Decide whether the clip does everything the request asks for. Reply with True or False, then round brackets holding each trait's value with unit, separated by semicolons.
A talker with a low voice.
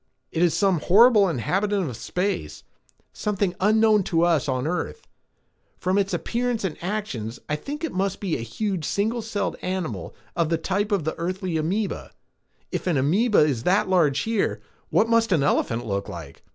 False (185 Hz)